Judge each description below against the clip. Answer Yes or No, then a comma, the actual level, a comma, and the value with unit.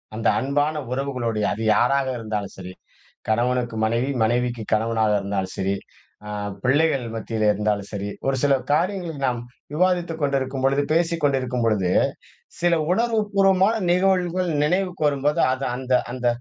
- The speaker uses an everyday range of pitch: No, wide, 6.3 semitones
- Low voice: Yes, low, 130 Hz